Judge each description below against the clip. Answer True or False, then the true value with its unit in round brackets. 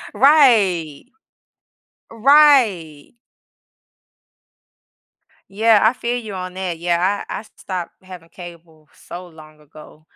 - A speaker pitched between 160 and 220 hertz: True (185 Hz)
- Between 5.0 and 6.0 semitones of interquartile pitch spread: True (5.3 semitones)